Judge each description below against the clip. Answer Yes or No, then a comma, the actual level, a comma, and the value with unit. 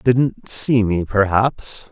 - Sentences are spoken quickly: No, slow, 125 wpm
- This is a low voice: Yes, low, 110 Hz